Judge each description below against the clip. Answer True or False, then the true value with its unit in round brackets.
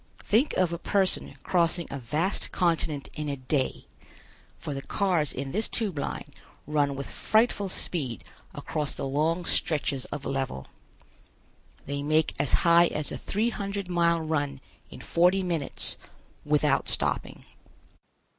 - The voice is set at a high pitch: False (155 Hz)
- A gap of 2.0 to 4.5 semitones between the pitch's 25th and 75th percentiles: True (4.1 semitones)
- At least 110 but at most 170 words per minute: True (140 wpm)